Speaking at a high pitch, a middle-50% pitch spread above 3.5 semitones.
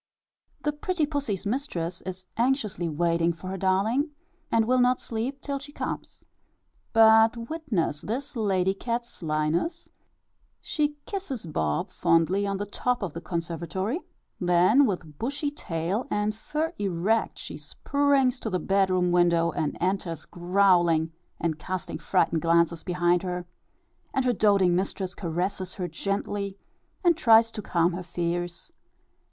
Yes: high, 195 Hz; wide, 5.6 semitones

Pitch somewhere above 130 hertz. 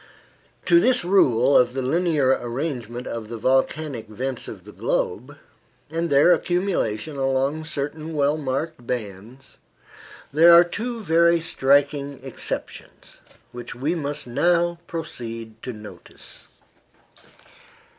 Yes: medium, 140 Hz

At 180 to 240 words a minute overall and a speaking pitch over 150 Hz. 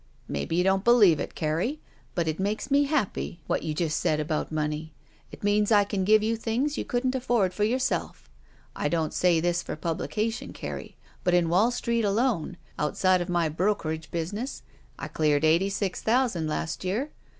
Yes: average, 200 wpm; medium, 185 Hz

